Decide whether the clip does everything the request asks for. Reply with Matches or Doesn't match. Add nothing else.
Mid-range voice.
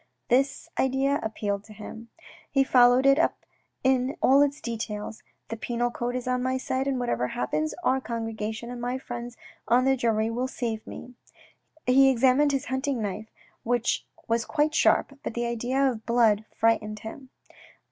Doesn't match